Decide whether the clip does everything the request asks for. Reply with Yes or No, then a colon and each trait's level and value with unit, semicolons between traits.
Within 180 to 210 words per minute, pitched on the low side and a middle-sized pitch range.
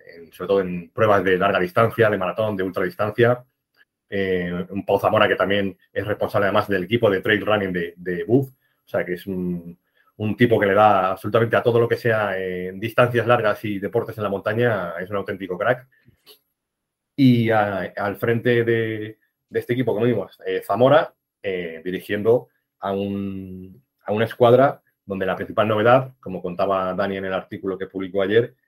Yes: average, 185 wpm; low, 100 Hz; average, 3.7 semitones